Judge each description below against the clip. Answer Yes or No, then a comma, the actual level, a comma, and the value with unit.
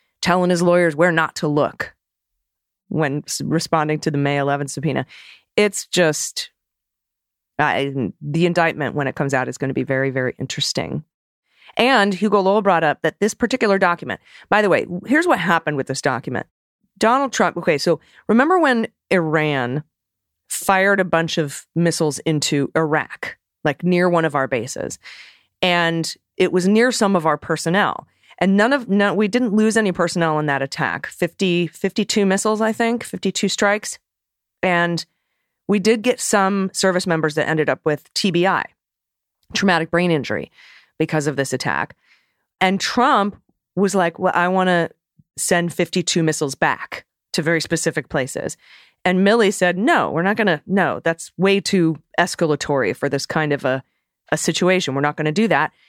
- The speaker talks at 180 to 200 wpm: No, average, 165 wpm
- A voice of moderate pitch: Yes, medium, 170 Hz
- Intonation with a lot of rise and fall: No, average, 4.3 semitones